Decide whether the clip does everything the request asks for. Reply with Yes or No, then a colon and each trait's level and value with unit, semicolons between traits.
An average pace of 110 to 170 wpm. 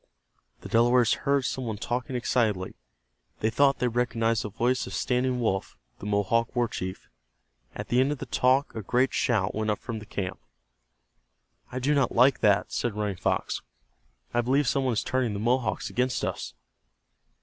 No: average, 180 wpm